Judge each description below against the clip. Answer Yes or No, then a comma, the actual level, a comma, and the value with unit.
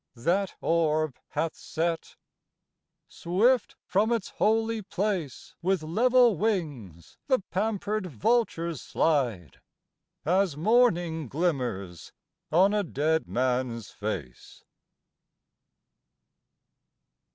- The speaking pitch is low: No, medium, 170 Hz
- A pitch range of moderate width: No, wide, 7.0 semitones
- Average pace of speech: No, slow, 85 wpm